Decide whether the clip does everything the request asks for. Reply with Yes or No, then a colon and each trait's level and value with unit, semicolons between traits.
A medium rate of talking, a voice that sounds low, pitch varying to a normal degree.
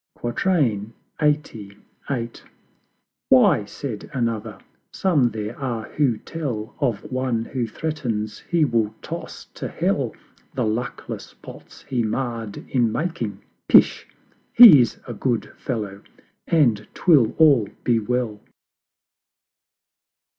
No: slow, 105 wpm; low, 120 Hz; average, 4.2 semitones